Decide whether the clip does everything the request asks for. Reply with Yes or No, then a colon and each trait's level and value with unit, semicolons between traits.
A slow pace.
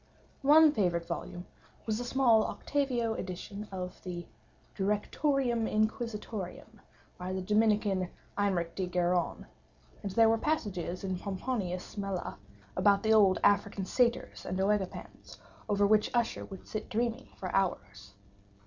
Yes: slow, 130 wpm